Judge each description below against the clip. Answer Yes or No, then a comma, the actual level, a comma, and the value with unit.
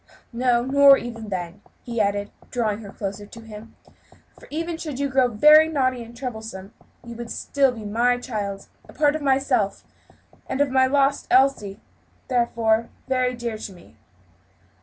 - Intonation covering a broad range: No, average, 3.9 semitones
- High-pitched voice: Yes, high, 240 Hz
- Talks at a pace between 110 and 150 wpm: No, average, 165 wpm